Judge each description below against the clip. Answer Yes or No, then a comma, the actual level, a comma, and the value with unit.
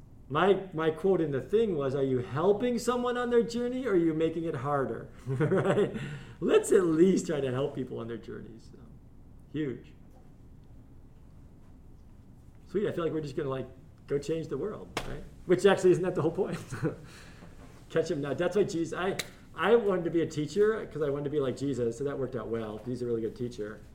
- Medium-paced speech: No, fast, 210 wpm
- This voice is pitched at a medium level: Yes, medium, 155 Hz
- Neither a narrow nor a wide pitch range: No, wide, 6.6 semitones